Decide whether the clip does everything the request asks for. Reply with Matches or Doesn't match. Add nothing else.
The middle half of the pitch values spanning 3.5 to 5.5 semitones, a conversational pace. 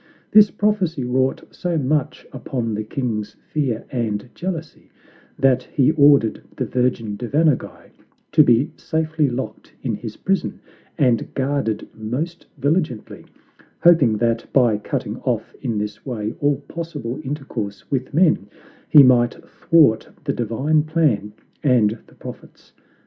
Doesn't match